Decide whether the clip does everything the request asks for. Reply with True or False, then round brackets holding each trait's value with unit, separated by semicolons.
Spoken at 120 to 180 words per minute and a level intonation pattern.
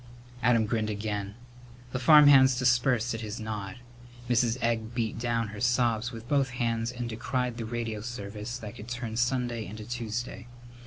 True (160 wpm; 1.9 semitones)